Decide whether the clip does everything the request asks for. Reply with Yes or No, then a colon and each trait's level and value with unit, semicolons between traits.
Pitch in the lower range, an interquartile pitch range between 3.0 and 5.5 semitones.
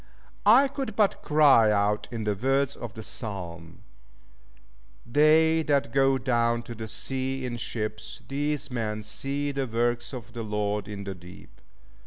Yes: low, 120 Hz; average, 4.6 semitones